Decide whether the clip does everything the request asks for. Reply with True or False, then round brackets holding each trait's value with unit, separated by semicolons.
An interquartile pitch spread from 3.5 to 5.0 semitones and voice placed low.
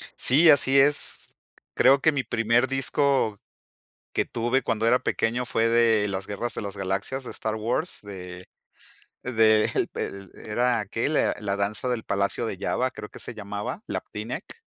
True (4.0 semitones; 115 Hz)